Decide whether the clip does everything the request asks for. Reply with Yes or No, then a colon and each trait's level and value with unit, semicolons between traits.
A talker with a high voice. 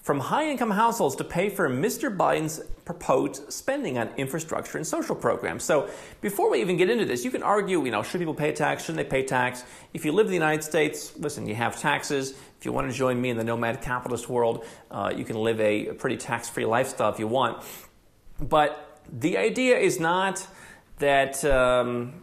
No: medium, 140 Hz